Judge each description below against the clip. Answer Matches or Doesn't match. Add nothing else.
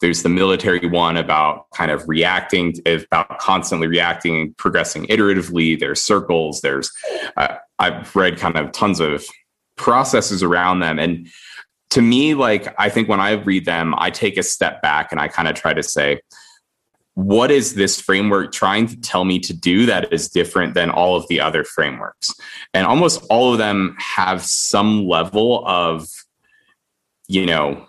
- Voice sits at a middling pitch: Doesn't match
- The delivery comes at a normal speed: Matches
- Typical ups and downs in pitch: Matches